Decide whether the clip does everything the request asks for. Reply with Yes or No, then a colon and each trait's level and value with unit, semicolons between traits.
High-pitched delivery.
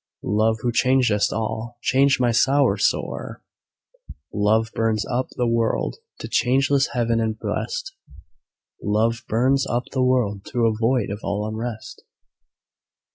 No: low, 115 Hz